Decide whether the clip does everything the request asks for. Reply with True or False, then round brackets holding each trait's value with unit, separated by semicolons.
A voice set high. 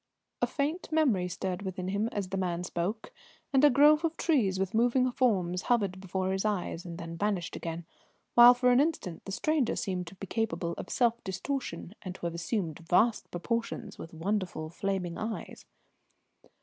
True (195 Hz)